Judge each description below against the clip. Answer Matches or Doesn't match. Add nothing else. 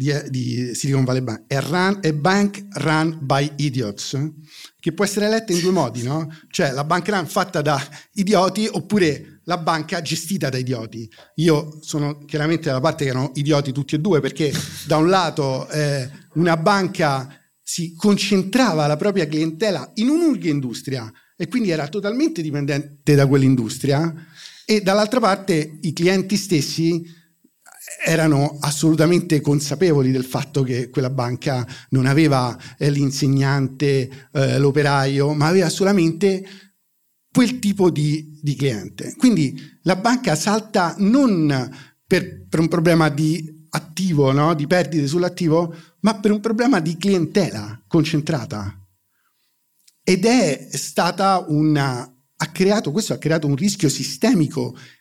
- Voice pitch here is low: Doesn't match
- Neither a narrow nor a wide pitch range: Matches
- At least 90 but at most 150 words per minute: Matches